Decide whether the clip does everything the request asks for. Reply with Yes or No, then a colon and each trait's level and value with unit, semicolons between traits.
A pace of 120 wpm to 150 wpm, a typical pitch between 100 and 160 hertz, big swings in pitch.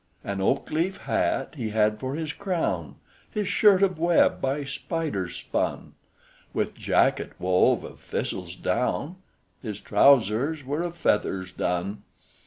Yes: slow, 135 wpm; medium, 140 Hz; wide, 8.2 semitones